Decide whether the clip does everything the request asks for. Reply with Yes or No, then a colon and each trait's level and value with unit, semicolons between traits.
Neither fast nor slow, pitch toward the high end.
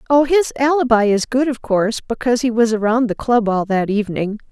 No: fast, 215 wpm; high, 235 Hz